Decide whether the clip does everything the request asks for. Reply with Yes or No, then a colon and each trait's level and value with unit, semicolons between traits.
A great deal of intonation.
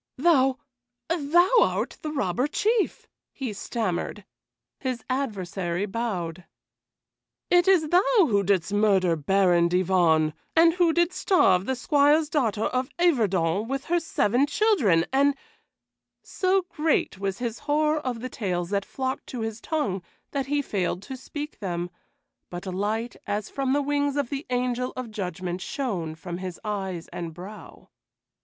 Yes: wide, 7.5 semitones